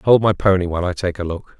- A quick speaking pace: Yes, fast, 300 wpm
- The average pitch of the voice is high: No, very low, 95 Hz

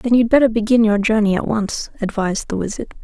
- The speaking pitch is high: Yes, high, 215 Hz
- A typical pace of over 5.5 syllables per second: Yes, 6.0 syllables/s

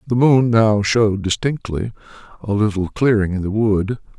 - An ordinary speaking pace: Yes, average, 160 wpm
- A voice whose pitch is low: Yes, low, 110 Hz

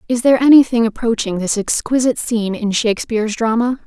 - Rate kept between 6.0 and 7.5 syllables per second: Yes, 6.4 syllables/s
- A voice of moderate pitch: No, high, 230 Hz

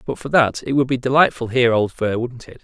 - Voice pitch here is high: No, low, 125 Hz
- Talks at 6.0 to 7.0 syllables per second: Yes, 6.1 syllables/s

